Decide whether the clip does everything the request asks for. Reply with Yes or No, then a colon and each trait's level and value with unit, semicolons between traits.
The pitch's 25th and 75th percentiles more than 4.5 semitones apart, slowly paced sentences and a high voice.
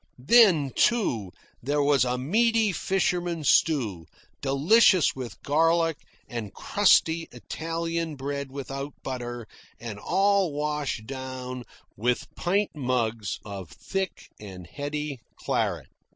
No: average, 5.1 semitones; slow, 110 wpm; medium, 145 Hz